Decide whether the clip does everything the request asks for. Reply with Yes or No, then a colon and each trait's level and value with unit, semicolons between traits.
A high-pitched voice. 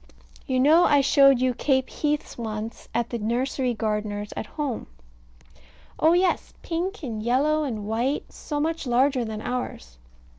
Yes: very high, 255 Hz